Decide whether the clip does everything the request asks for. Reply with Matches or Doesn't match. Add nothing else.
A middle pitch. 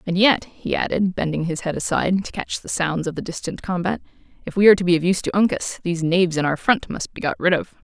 Matches